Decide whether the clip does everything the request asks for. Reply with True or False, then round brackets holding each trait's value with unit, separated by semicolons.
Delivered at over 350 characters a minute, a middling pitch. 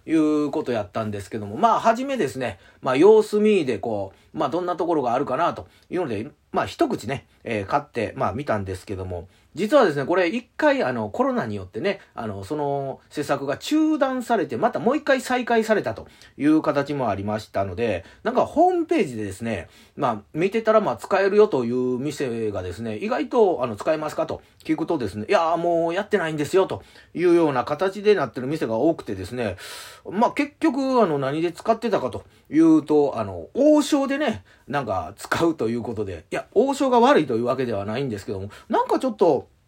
True (405 characters per minute; 165 Hz)